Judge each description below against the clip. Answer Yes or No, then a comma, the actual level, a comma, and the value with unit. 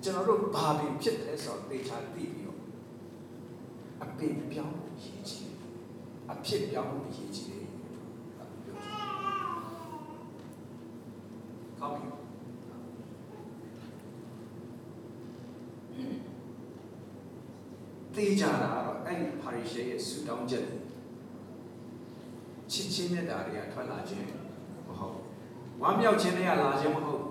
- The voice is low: Yes, low, 120 Hz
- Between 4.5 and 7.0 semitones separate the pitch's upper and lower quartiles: Yes, average, 5.2 semitones